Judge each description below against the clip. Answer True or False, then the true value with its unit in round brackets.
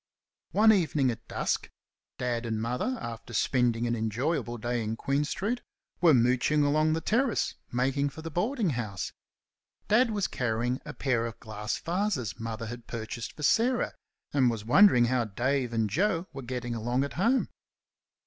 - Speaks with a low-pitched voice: True (125 Hz)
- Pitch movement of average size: False (5.8 semitones)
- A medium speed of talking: True (160 wpm)